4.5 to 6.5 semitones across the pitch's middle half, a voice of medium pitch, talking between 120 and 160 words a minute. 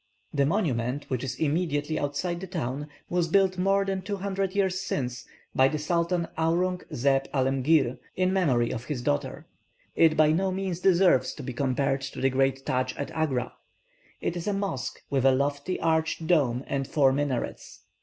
No: average, 5.2 semitones; medium, 150 Hz; average, 175 wpm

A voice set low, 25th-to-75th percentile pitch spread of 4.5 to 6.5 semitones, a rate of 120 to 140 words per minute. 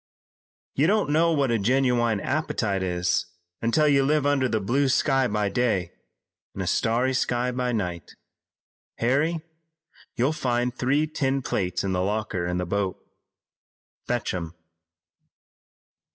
Yes: low, 120 Hz; wide, 5.6 semitones; slow, 135 wpm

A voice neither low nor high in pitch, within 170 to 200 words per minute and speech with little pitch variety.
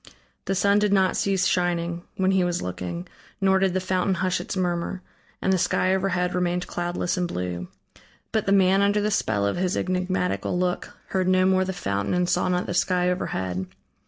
Yes: medium, 180 Hz; average, 195 wpm; narrow, 1.4 semitones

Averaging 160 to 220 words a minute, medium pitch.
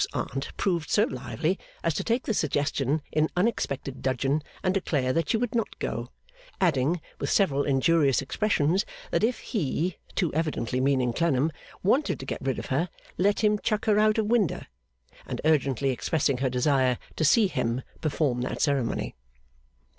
Yes: average, 170 wpm; medium, 155 Hz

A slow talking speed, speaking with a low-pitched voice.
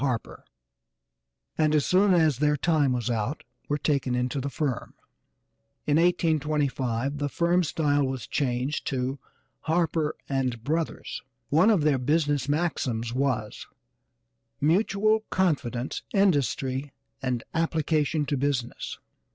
No: slow, 120 wpm; medium, 145 Hz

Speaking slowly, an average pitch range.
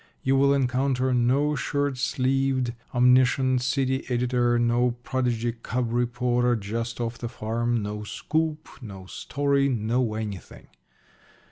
No: slow, 120 wpm; narrow, 2.0 semitones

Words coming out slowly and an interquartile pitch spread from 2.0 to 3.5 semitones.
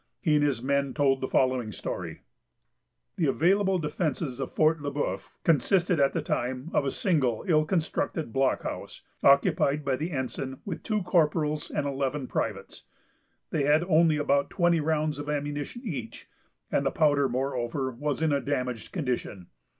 No: average, 160 wpm; average, 3.0 semitones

